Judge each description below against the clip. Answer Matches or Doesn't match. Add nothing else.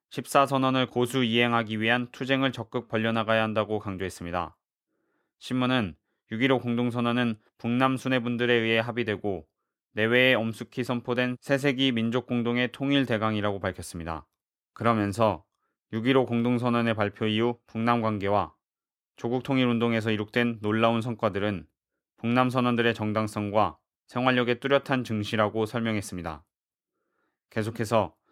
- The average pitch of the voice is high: Doesn't match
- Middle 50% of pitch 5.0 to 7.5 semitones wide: Doesn't match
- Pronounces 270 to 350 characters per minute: Matches